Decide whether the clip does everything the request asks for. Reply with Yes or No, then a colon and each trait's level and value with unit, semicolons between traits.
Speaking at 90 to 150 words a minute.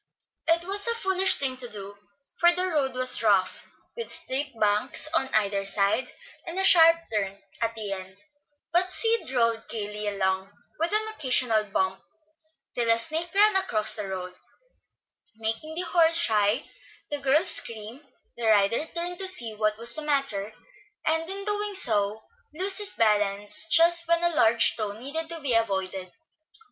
No: average, 165 wpm